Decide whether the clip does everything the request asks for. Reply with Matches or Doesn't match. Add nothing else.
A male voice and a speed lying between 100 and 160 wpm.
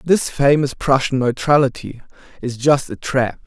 Matches